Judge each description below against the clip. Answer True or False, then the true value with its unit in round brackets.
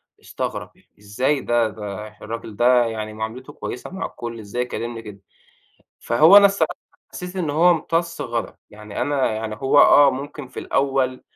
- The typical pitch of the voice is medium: False (125 Hz)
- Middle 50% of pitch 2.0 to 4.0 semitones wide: False (4.7 semitones)